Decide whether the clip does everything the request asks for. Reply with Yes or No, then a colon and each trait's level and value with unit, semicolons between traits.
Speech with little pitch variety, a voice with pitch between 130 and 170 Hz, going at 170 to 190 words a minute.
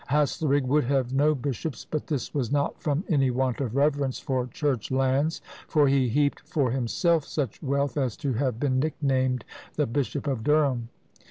Yes: narrow, 2.2 semitones; low, 135 Hz; average, 175 wpm